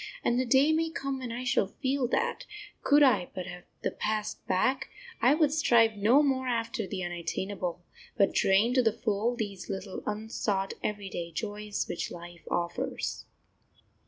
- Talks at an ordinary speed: Yes, average, 160 wpm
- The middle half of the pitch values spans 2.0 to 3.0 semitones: No, average, 5.2 semitones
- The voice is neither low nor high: No, high, 220 Hz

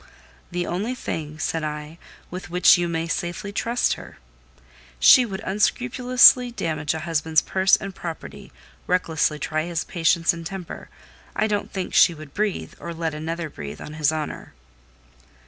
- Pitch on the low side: No, medium, 170 Hz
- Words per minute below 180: Yes, average, 155 wpm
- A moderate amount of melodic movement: Yes, average, 3.5 semitones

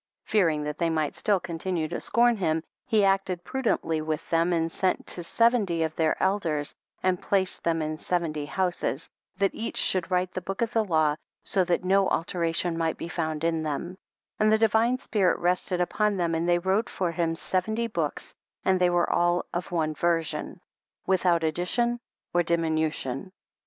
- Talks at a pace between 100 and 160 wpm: No, average, 180 wpm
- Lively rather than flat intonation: No, average, 2.9 semitones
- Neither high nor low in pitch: Yes, medium, 175 Hz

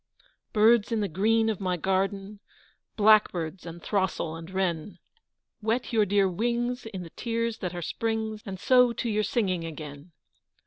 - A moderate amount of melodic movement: Yes, average, 3.8 semitones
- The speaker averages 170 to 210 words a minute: No, average, 160 wpm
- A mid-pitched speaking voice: No, high, 200 Hz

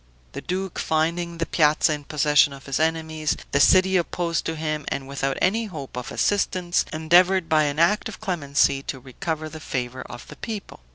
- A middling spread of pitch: Yes, average, 3.6 semitones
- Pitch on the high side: No, medium, 160 Hz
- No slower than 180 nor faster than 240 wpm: Yes, average, 185 wpm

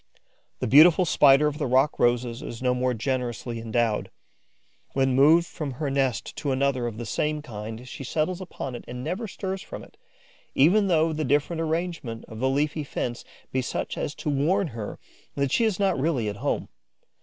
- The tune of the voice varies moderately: Yes, average, 4.4 semitones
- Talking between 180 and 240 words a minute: Yes, average, 190 wpm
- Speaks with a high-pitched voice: No, medium, 140 Hz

